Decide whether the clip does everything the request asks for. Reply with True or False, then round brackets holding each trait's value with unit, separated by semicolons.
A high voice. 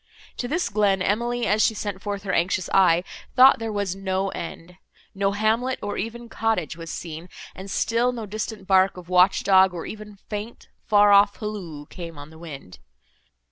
True (200 Hz)